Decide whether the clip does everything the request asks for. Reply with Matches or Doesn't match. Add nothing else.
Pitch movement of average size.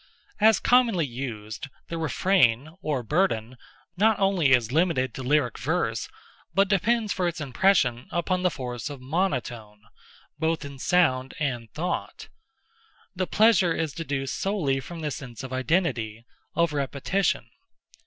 Doesn't match